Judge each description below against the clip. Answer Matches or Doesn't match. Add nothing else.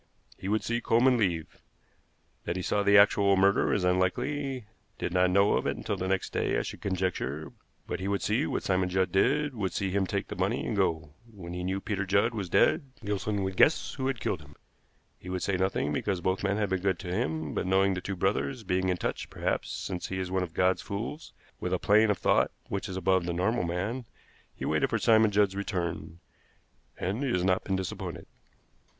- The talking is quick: Matches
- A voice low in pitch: Matches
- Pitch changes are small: Matches